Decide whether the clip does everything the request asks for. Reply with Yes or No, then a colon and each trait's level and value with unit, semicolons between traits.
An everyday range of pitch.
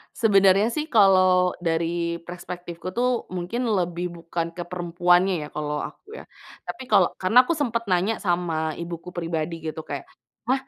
Yes: average, 3.2 semitones